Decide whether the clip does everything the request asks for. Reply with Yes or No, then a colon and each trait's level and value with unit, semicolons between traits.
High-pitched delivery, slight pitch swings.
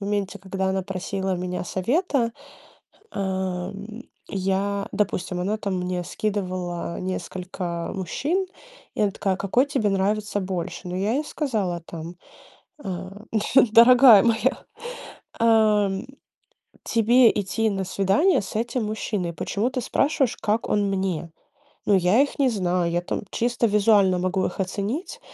No: high, 200 Hz; average, 3.3 semitones